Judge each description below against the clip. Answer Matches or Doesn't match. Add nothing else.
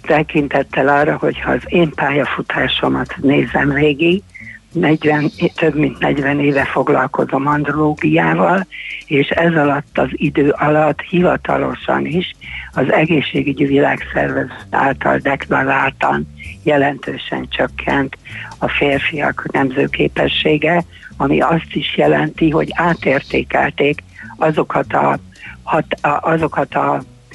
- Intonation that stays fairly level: Matches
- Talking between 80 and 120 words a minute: Matches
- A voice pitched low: Doesn't match